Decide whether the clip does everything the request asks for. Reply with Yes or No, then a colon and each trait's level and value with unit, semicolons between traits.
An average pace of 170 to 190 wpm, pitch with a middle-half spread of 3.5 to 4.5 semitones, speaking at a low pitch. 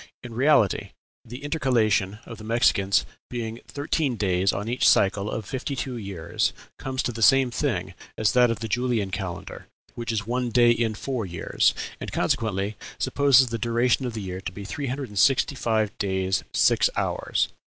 Yes: average, 180 wpm; average, 3.9 semitones; low, 115 Hz